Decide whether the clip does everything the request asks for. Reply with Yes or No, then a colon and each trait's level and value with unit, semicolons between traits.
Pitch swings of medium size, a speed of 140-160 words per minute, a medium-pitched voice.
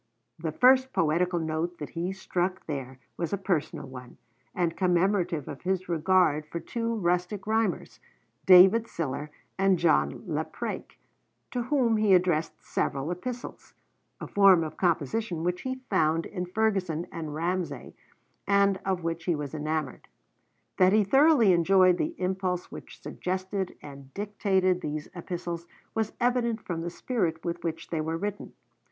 Yes: average, 3.5 semitones; average, 145 wpm; medium, 180 Hz